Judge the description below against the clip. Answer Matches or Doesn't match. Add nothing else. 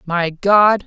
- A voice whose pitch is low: Doesn't match